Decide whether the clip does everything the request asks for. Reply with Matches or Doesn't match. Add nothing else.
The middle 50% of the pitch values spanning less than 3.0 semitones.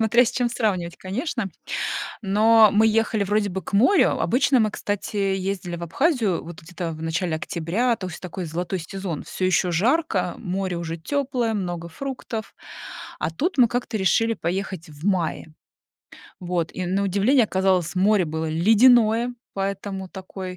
Doesn't match